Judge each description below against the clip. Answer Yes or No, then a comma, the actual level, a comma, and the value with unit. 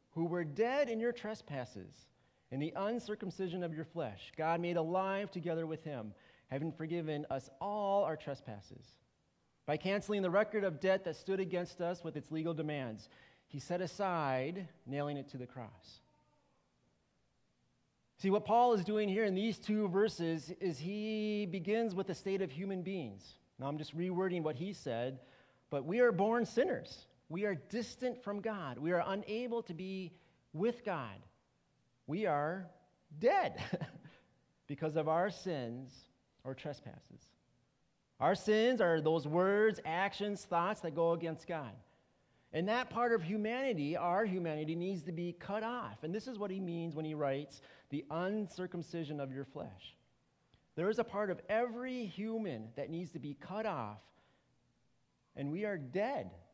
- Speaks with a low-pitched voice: No, medium, 175 Hz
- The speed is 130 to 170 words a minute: Yes, average, 160 wpm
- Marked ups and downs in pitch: Yes, wide, 5.8 semitones